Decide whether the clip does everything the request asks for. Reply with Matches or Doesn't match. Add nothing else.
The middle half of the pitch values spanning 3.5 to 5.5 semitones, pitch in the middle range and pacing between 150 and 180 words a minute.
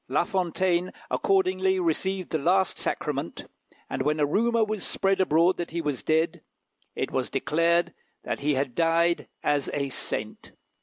Matches